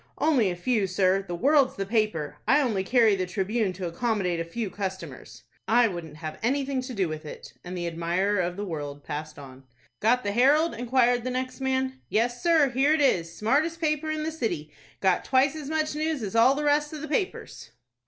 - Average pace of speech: No, fast, 210 wpm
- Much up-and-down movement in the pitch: Yes, wide, 7.1 semitones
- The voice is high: Yes, high, 230 Hz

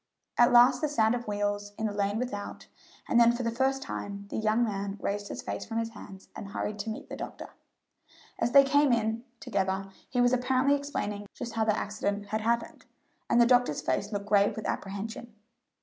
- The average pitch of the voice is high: Yes, high, 220 Hz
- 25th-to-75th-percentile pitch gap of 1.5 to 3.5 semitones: Yes, average, 3.0 semitones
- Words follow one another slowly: No, fast, 205 wpm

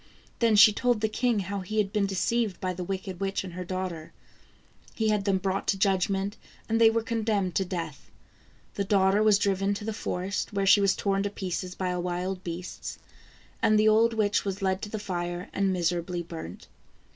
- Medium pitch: No, high, 195 Hz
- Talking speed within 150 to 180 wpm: No, average, 200 wpm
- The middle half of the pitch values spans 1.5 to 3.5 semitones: Yes, narrow, 2.4 semitones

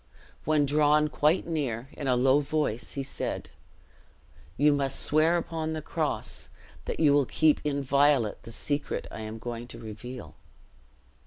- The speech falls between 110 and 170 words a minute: Yes, average, 150 wpm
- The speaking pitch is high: No, medium, 140 Hz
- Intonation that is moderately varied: Yes, average, 3.7 semitones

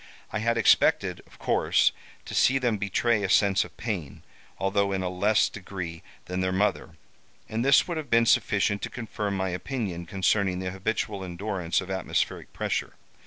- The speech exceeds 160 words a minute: Yes, average, 170 wpm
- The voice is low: Yes, low, 100 Hz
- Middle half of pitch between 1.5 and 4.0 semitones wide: Yes, average, 3.0 semitones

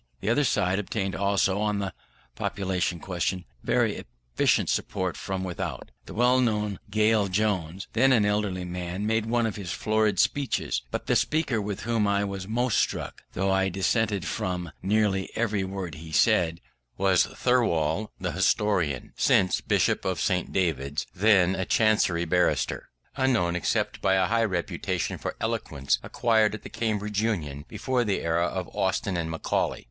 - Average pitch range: Yes, average, 3.2 semitones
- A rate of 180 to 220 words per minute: No, average, 160 wpm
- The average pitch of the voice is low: Yes, very low, 95 Hz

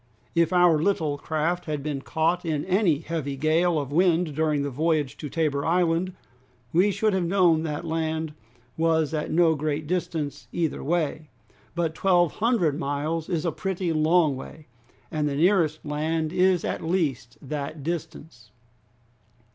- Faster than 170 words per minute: No, average, 155 wpm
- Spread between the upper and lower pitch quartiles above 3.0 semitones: No, narrow, 2.5 semitones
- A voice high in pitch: No, medium, 160 Hz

